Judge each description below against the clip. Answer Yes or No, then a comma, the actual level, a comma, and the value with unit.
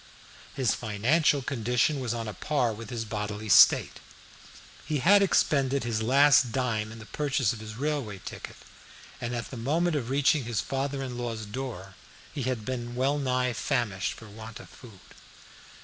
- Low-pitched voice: Yes, low, 125 Hz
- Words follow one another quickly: No, average, 170 wpm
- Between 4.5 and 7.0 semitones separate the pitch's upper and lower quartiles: No, average, 3.8 semitones